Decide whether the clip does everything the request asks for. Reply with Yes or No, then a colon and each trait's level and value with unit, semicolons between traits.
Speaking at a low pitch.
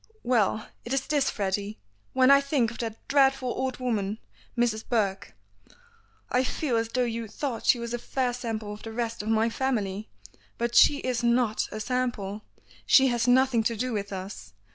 No: high, 235 Hz